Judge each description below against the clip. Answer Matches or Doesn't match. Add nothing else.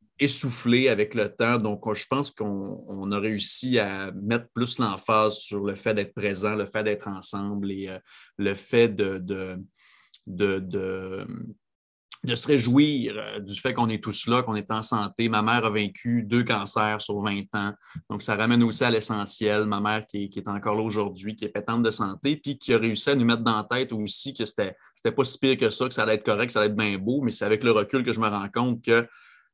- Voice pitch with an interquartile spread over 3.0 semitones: Doesn't match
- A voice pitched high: Doesn't match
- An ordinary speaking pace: Doesn't match